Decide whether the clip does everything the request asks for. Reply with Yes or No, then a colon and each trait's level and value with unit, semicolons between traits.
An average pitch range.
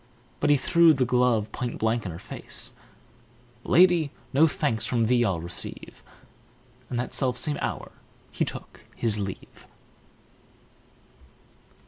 Yes: average, 4.8 semitones